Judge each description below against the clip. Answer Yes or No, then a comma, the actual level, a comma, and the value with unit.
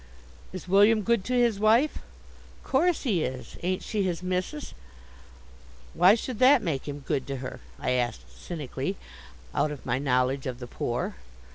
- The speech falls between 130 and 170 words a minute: Yes, average, 160 wpm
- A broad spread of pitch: Yes, wide, 8.4 semitones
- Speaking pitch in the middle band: Yes, medium, 180 Hz